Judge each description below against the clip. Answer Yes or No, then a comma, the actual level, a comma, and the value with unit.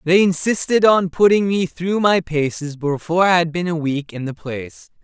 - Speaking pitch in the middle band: Yes, medium, 165 Hz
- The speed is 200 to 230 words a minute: Yes, fast, 205 wpm